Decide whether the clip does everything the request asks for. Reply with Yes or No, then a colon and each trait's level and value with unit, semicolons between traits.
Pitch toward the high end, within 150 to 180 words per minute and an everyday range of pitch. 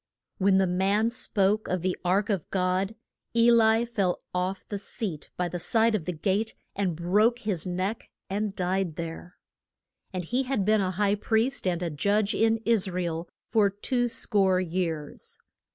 Yes: high, 195 Hz; average, 175 wpm; average, 3.4 semitones